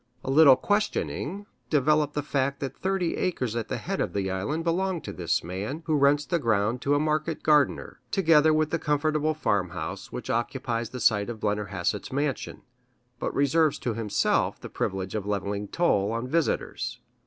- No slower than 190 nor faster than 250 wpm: No, average, 175 wpm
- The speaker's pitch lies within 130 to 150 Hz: Yes, medium, 140 Hz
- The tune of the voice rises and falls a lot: Yes, wide, 6.5 semitones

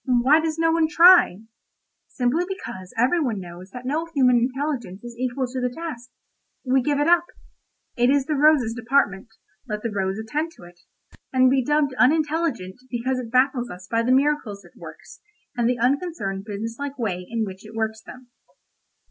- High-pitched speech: Yes, very high, 250 Hz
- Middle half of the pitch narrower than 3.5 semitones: No, average, 4.9 semitones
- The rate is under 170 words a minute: No, average, 180 wpm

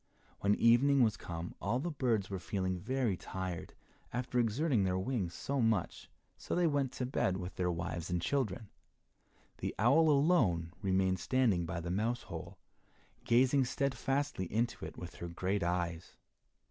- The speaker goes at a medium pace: Yes, average, 160 wpm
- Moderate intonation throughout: No, wide, 6.3 semitones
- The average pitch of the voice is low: Yes, low, 105 Hz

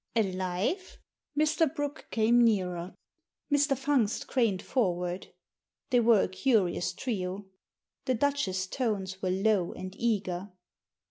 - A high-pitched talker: Yes, high, 210 Hz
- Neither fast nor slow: No, slow, 120 wpm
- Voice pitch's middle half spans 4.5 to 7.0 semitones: Yes, wide, 5.5 semitones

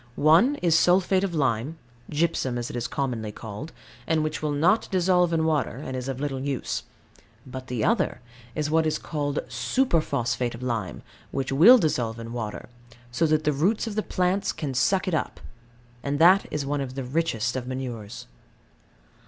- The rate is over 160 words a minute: Yes, average, 180 wpm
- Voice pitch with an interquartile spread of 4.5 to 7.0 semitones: Yes, average, 4.9 semitones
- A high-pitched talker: No, medium, 145 Hz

